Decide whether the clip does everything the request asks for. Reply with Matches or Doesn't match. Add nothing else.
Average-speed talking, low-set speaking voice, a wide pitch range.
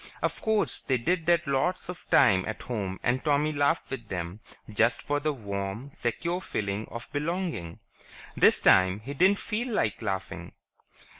Matches